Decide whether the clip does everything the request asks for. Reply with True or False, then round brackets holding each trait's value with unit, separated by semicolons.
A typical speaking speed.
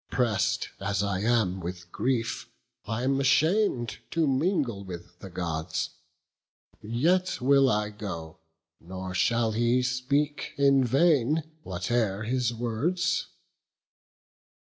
False (110 wpm)